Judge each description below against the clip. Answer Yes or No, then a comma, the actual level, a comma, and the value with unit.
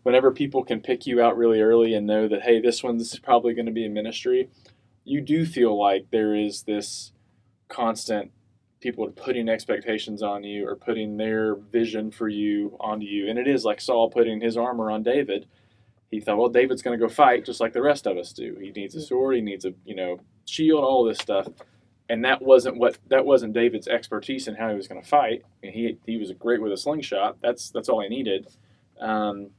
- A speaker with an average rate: No, fast, 225 wpm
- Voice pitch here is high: No, low, 115 Hz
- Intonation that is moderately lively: No, narrow, 2.3 semitones